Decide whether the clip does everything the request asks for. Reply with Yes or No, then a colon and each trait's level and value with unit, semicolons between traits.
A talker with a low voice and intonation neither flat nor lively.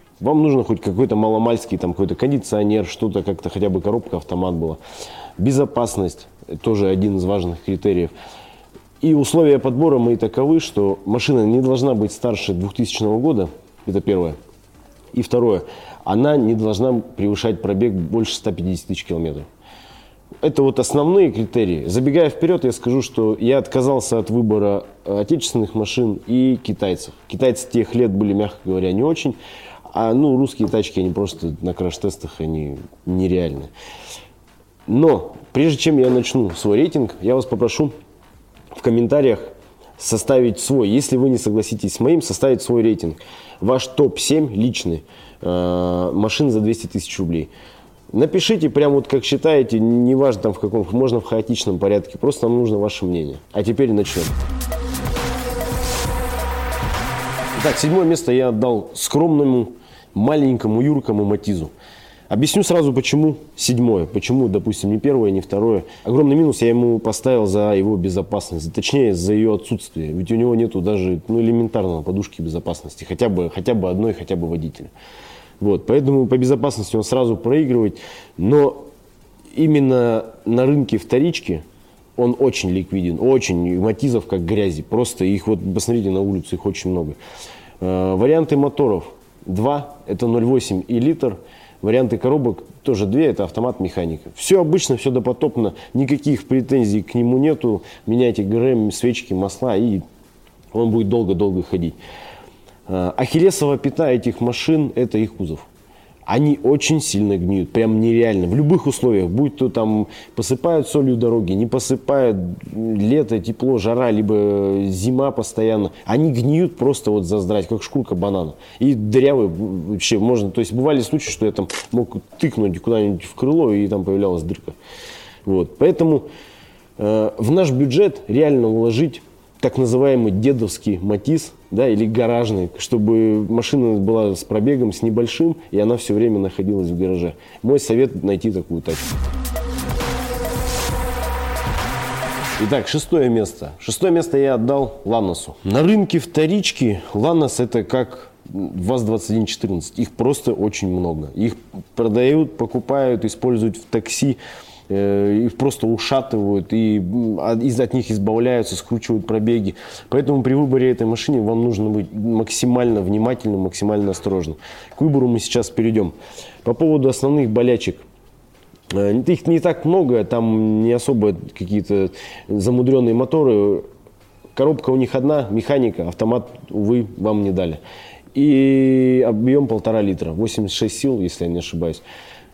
Yes: low, 115 Hz; average, 4.7 semitones